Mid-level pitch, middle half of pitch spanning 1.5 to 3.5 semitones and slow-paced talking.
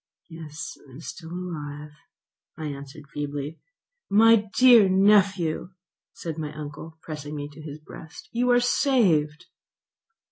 No: medium, 160 Hz; average, 5.0 semitones; slow, 130 wpm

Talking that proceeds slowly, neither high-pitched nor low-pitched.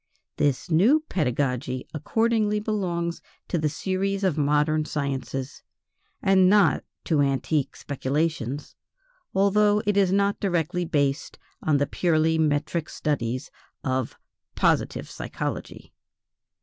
Yes: slow, 110 wpm; medium, 155 Hz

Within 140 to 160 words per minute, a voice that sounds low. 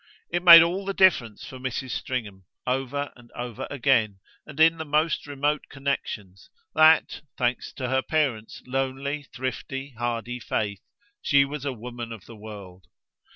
Yes: average, 155 wpm; low, 130 Hz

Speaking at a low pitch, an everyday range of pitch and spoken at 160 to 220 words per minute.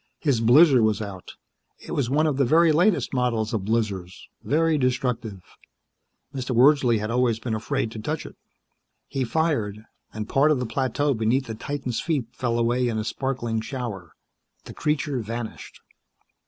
Yes: low, 125 Hz; average, 3.9 semitones; average, 165 wpm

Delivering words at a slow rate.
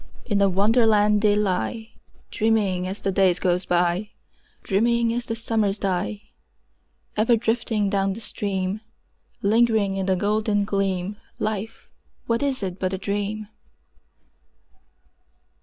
Yes: slow, 125 wpm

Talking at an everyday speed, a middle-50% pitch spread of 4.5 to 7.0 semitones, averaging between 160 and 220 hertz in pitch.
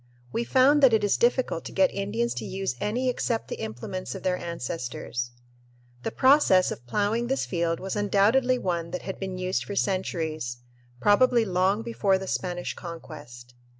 Yes: average, 170 wpm; average, 5.2 semitones; high, 190 Hz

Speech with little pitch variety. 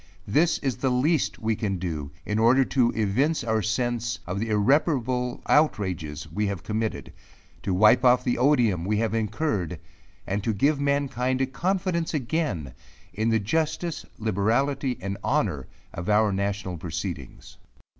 No: average, 5.3 semitones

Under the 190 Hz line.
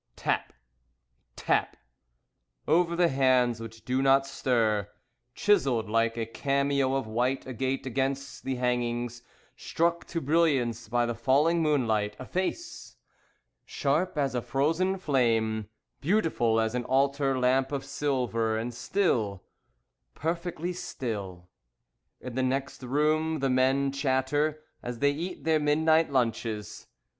Yes: low, 135 Hz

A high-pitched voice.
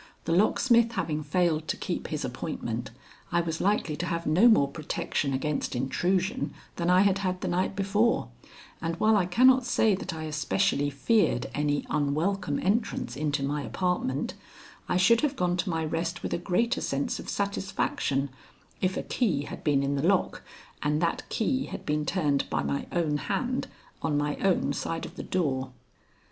No: medium, 170 Hz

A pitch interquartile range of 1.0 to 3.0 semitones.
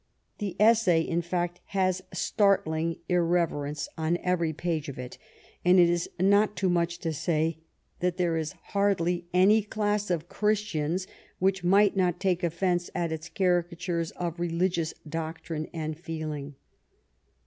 Yes: narrow, 2.4 semitones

